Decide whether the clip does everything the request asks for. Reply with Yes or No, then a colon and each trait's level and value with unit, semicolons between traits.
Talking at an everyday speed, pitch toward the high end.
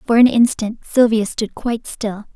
Yes: average, 180 wpm; high, 225 Hz